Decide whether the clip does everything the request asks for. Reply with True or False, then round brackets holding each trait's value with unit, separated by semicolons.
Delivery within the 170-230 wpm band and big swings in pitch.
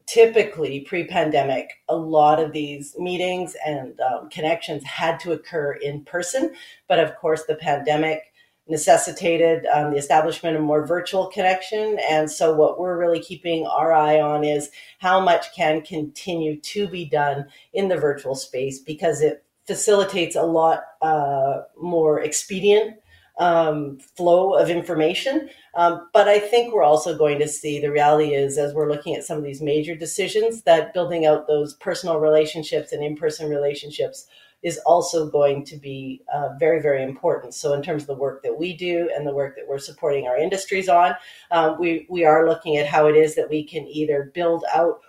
False (180 wpm; 2.8 semitones)